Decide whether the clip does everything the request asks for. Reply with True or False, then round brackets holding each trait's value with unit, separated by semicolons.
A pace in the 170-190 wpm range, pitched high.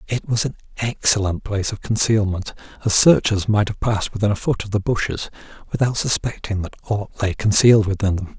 False (185 wpm; 105 Hz)